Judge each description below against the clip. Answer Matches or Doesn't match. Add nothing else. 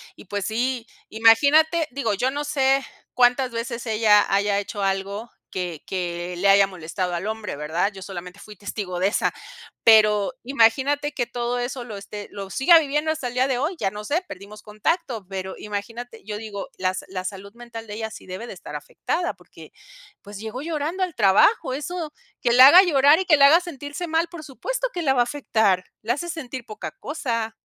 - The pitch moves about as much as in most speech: Doesn't match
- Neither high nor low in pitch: Doesn't match